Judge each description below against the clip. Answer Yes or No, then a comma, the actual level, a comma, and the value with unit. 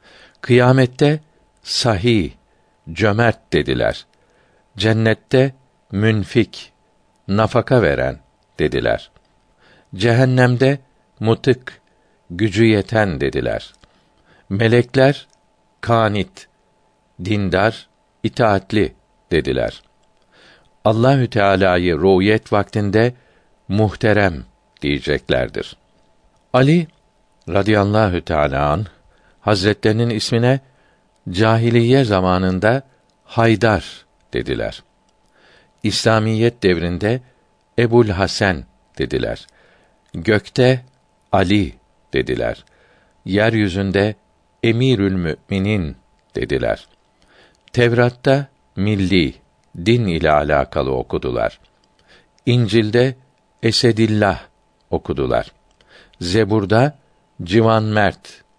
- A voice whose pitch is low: Yes, low, 110 Hz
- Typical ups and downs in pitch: Yes, average, 3.6 semitones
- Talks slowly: Yes, slow, 60 wpm